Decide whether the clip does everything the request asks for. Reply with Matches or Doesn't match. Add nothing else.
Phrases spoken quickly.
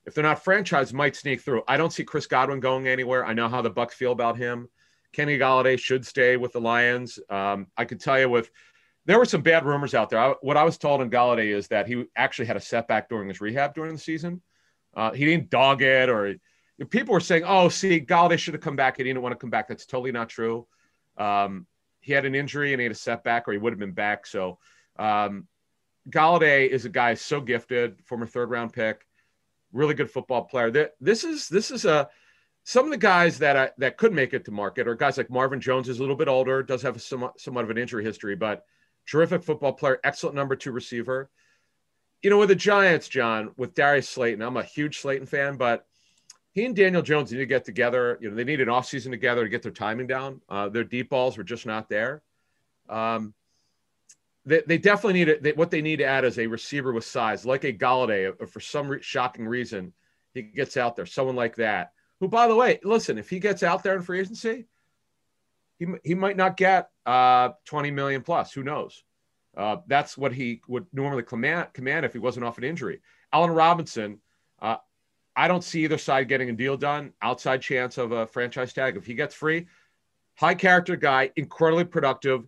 Matches